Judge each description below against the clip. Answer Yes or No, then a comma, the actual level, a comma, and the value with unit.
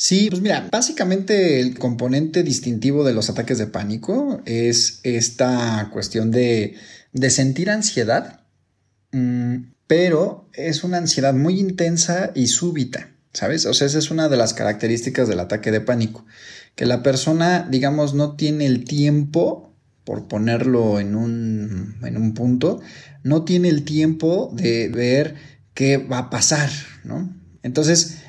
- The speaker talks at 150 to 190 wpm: No, average, 140 wpm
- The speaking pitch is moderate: No, low, 130 Hz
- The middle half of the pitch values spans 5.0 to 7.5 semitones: Yes, wide, 5.4 semitones